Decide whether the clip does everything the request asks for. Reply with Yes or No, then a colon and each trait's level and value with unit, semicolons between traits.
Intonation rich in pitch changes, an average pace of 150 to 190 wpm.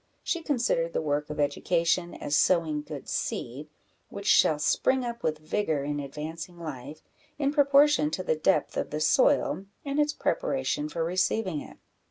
Yes: wide, 7.8 semitones; average, 165 wpm